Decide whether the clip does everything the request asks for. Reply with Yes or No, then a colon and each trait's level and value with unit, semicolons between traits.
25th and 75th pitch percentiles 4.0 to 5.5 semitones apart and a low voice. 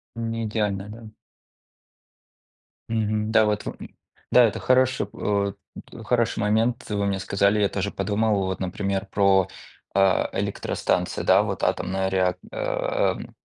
No: narrow, 2.5 semitones; low, 105 Hz